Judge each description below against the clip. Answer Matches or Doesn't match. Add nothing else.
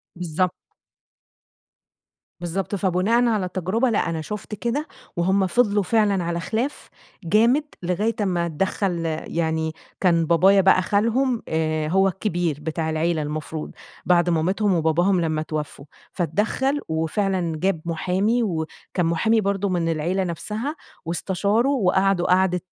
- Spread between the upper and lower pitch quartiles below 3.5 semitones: Doesn't match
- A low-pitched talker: Doesn't match